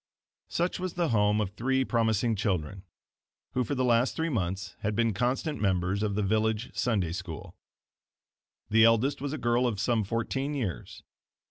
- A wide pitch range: No, average, 4.1 semitones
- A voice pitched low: Yes, low, 110 Hz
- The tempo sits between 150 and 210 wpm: Yes, average, 165 wpm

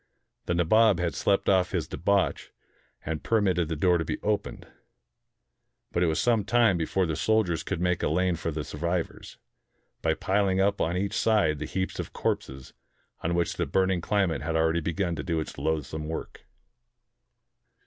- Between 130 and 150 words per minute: No, average, 180 wpm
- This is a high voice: No, very low, 85 Hz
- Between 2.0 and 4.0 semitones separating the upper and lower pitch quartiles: Yes, average, 3.4 semitones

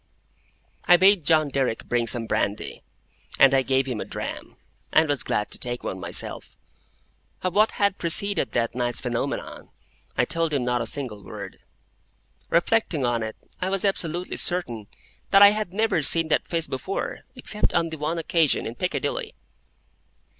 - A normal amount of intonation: No, wide, 6.7 semitones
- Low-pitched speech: No, medium, 150 Hz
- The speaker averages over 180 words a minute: No, average, 165 wpm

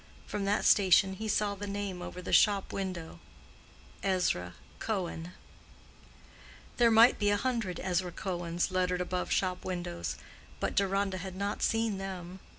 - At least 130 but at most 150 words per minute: Yes, average, 140 wpm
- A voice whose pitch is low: No, high, 190 Hz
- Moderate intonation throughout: No, narrow, 2.2 semitones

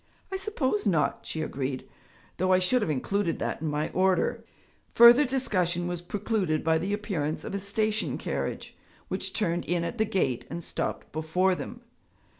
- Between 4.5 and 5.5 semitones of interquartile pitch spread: Yes, average, 4.8 semitones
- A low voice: No, medium, 185 Hz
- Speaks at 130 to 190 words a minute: Yes, average, 170 wpm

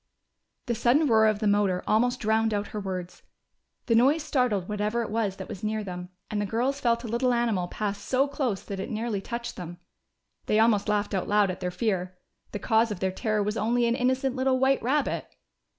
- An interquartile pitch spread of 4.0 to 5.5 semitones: No, average, 2.9 semitones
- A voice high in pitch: Yes, high, 220 Hz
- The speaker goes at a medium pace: No, fast, 215 wpm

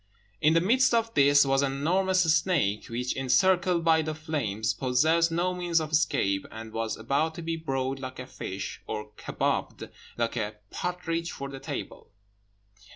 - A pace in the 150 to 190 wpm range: Yes, average, 165 wpm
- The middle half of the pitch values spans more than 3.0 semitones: Yes, average, 5.0 semitones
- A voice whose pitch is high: No, medium, 145 Hz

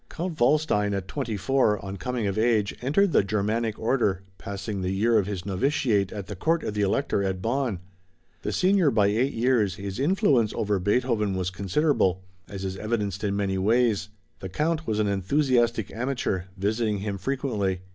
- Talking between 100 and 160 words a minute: No, average, 175 wpm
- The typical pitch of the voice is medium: No, low, 105 Hz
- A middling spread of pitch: Yes, average, 4.4 semitones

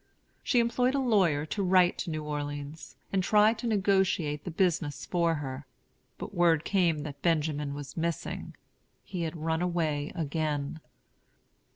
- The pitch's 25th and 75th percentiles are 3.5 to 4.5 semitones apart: Yes, average, 4.1 semitones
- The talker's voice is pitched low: No, medium, 165 Hz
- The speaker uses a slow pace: No, average, 150 wpm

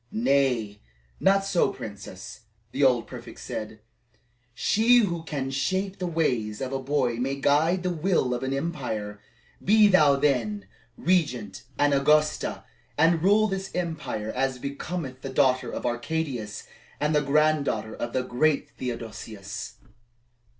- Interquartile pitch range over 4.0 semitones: Yes, average, 5.2 semitones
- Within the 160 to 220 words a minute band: No, slow, 135 wpm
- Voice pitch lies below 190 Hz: Yes, medium, 140 Hz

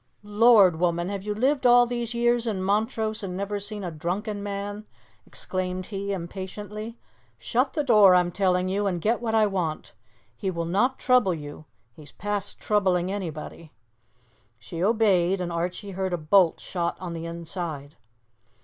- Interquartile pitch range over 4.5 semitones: No, average, 3.4 semitones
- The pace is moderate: Yes, average, 160 wpm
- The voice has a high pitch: Yes, high, 195 Hz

